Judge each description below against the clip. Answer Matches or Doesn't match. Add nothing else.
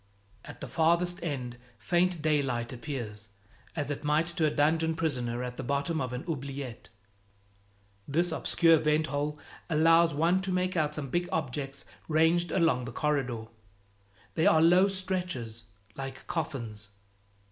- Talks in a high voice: Doesn't match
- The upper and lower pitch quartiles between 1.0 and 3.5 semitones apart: Doesn't match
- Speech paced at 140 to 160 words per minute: Matches